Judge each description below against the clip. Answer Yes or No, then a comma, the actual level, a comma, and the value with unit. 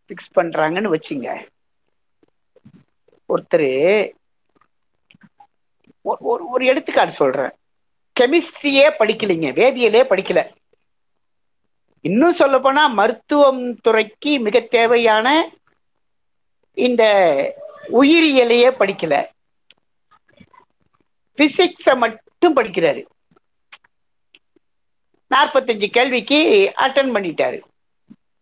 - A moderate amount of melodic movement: No, wide, 6.6 semitones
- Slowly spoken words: Yes, slow, 60 wpm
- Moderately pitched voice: No, very high, 275 Hz